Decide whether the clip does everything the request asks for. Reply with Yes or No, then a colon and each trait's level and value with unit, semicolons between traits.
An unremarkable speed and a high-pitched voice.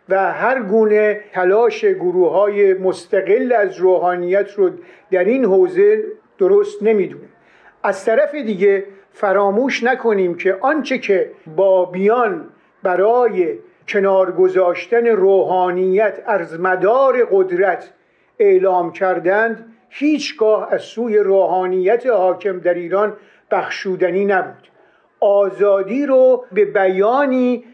No: slow, 95 wpm; high, 210 Hz